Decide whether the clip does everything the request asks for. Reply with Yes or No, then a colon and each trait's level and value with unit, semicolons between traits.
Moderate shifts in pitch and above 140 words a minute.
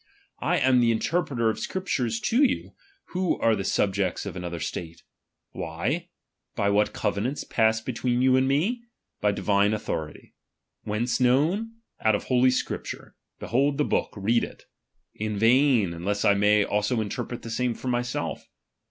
Yes: average, 4.2 semitones; average, 160 wpm